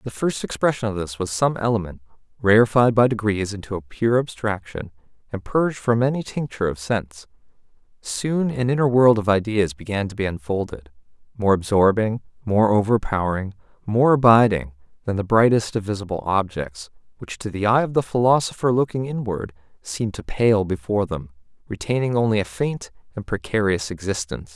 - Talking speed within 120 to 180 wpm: Yes, average, 160 wpm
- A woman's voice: No, male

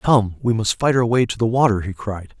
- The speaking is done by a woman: No, male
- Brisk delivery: Yes, fast, 275 wpm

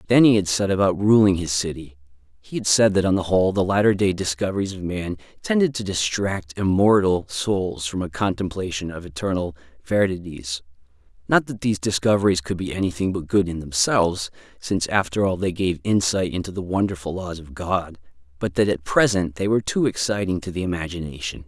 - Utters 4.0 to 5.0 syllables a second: No, 5.6 syllables/s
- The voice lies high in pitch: No, very low, 95 Hz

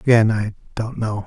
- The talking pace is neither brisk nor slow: Yes, average, 190 wpm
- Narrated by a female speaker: No, male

